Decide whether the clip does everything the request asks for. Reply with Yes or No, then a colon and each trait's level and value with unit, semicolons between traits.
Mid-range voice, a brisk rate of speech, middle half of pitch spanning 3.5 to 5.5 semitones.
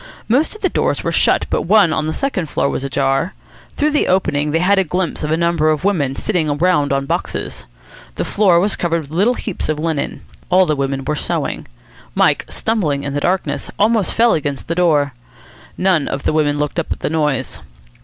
Yes: medium, 160 Hz; fast, 210 wpm; average, 4.6 semitones